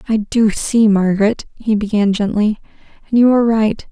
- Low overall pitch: No, high, 215 Hz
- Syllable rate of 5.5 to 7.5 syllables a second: No, 5.1 syllables/s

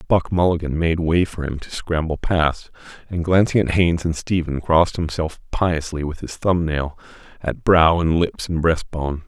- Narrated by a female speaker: No, male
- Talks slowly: No, average, 175 wpm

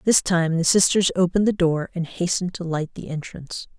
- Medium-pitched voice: Yes, medium, 175 Hz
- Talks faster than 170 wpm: Yes, fast, 205 wpm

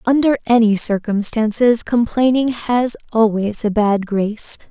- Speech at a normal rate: No, slow, 115 wpm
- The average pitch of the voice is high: Yes, high, 225 Hz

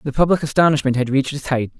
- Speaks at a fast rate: Yes, fast, 235 wpm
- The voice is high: No, medium, 140 Hz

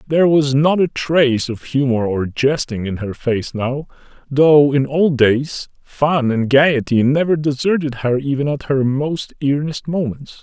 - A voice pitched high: No, medium, 140 Hz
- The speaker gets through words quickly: No, average, 165 wpm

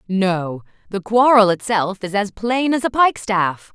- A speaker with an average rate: Yes, average, 145 wpm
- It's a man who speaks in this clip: No, female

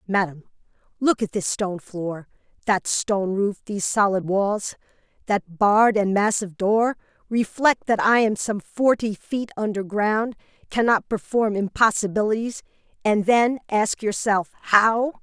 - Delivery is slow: Yes, slow, 130 wpm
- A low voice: No, high, 210 Hz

